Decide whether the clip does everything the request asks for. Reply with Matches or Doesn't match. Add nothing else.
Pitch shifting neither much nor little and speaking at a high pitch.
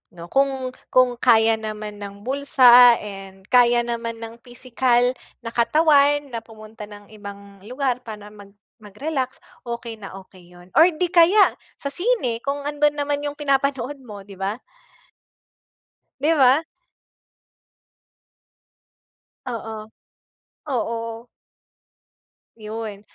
Matches